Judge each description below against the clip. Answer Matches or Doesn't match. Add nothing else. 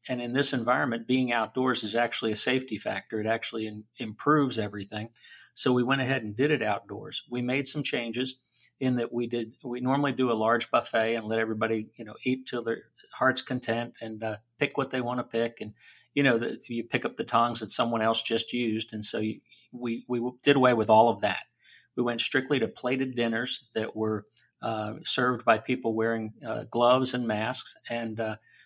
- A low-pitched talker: Matches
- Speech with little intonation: Matches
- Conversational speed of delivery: Doesn't match